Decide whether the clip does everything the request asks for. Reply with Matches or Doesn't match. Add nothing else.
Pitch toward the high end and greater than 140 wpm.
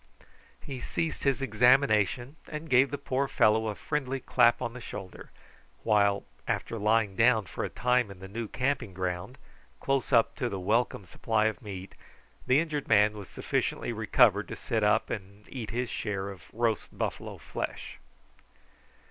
Doesn't match